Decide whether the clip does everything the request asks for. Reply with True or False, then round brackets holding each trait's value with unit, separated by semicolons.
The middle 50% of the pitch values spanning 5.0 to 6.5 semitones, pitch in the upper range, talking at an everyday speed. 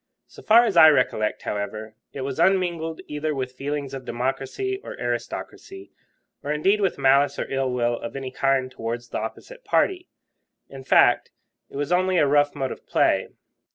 False (5.4 semitones; 140 Hz; 175 wpm)